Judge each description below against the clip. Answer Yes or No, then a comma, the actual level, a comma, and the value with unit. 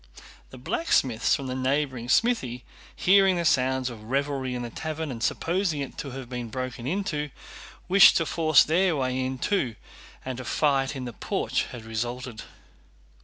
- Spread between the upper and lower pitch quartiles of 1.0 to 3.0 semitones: No, average, 4.0 semitones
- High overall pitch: No, low, 130 Hz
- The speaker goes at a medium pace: Yes, average, 170 wpm